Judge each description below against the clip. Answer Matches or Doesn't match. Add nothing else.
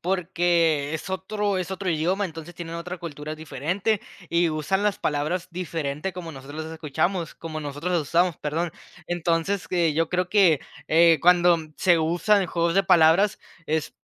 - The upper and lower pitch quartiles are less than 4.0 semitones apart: Matches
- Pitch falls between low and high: Matches